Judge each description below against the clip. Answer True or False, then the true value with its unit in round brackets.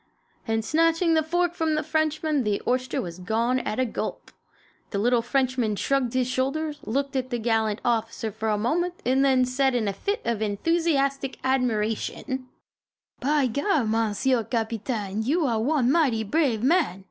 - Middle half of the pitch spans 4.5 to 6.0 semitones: True (4.9 semitones)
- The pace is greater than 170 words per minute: False (160 wpm)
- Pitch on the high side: True (255 Hz)